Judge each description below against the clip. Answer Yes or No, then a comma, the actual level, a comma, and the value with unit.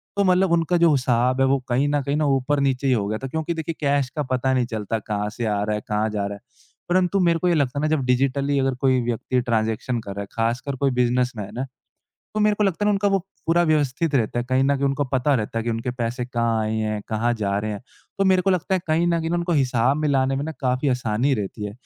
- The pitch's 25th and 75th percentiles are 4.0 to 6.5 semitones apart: Yes, average, 4.9 semitones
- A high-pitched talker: No, low, 130 Hz